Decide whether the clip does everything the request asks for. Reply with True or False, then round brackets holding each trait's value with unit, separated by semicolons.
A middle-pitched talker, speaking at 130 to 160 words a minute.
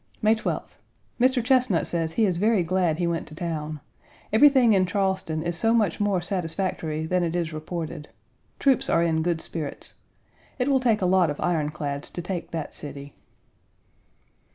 False (175 Hz; 175 wpm)